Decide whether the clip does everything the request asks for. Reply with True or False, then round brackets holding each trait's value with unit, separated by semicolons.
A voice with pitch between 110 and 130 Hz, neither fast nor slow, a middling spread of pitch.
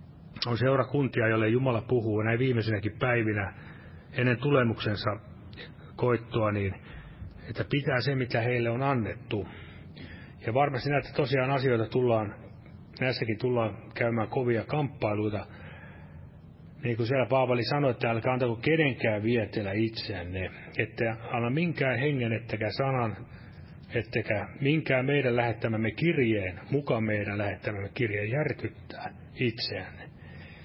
True (115 Hz; 115 wpm; 3.3 semitones)